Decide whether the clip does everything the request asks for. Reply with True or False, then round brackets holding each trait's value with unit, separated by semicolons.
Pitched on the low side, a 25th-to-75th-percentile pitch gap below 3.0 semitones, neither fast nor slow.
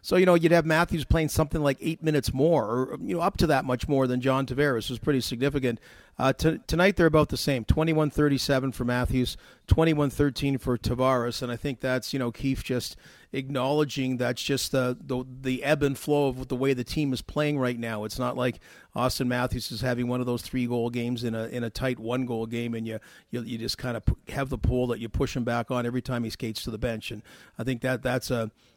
False (130 Hz; 2.5 semitones; 245 wpm)